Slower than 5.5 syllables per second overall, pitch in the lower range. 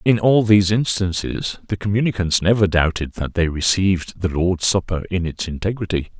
Yes: 5.3 syllables/s; very low, 95 Hz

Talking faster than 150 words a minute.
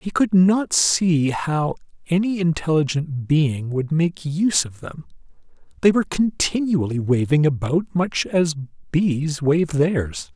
No: slow, 135 wpm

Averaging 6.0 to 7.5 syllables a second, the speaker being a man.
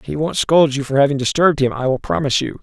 Yes: 6.7 syllables/s; male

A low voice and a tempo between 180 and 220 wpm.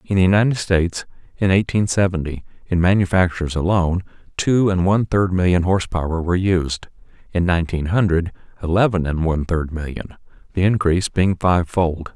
No: very low, 90 Hz; average, 160 wpm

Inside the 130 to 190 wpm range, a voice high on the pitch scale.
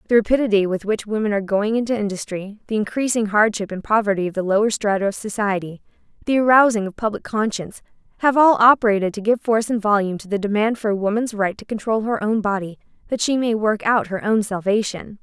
No: fast, 205 wpm; high, 210 Hz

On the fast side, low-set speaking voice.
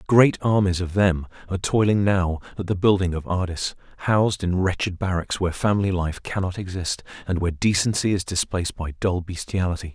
No: average, 175 wpm; very low, 95 Hz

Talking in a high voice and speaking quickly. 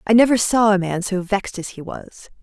Yes: high, 200 Hz; fast, 245 wpm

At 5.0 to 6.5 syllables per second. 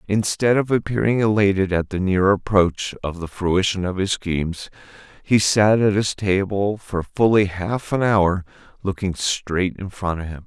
No: 4.4 syllables/s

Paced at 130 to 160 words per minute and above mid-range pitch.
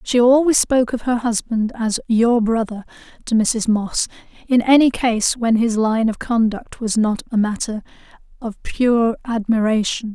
Yes: average, 155 wpm; high, 230 Hz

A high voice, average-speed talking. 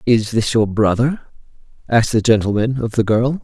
No: low, 115 Hz; average, 175 wpm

